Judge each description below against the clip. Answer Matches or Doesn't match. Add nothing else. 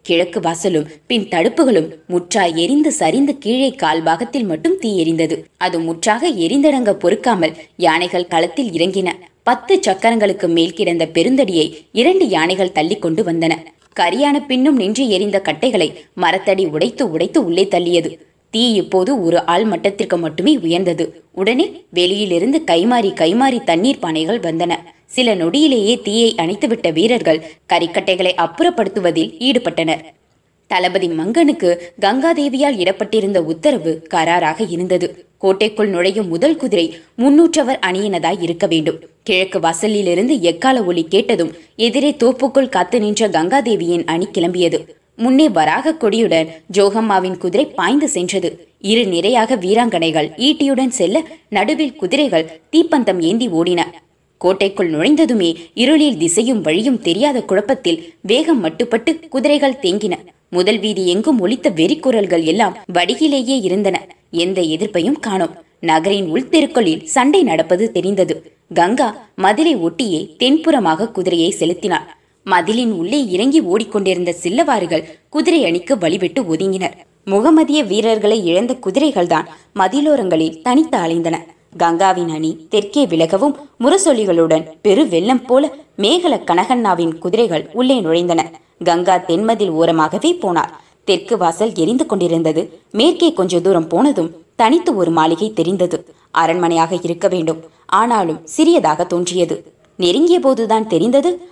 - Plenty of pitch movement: Matches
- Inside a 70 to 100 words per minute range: Doesn't match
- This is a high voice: Matches